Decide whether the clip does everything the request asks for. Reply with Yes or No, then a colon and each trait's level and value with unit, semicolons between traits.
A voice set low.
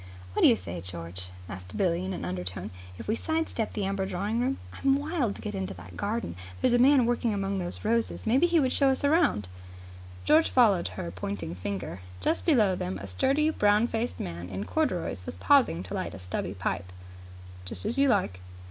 No: high, 195 Hz